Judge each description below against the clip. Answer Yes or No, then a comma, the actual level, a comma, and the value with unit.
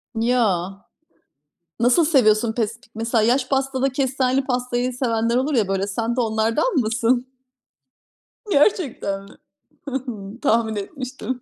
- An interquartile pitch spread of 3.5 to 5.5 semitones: No, average, 2.9 semitones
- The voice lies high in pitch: Yes, high, 240 Hz